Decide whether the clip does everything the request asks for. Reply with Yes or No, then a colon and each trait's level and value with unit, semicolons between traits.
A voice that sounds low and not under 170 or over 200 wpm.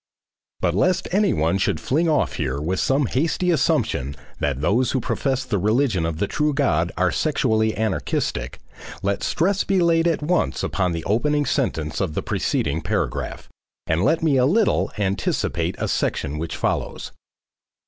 No: low, 110 Hz; average, 160 wpm